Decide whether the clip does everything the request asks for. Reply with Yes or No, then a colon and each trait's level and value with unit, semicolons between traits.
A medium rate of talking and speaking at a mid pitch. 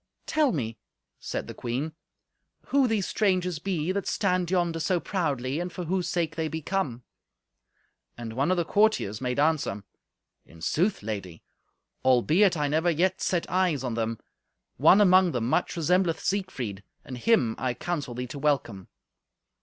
Yes: average, 160 wpm; medium, 160 Hz